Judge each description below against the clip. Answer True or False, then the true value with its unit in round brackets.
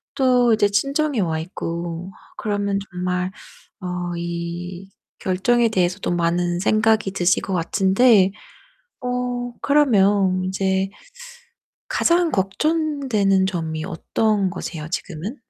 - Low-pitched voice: False (195 Hz)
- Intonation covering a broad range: False (4.3 semitones)